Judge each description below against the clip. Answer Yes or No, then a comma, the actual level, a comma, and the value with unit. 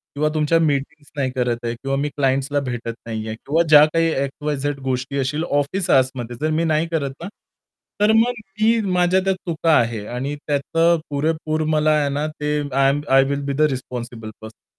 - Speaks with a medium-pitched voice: Yes, medium, 145 Hz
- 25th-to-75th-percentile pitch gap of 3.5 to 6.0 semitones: No, average, 3.0 semitones